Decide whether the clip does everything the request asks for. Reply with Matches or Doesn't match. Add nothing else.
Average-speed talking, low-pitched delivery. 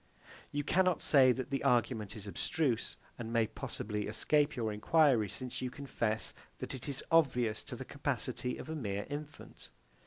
Matches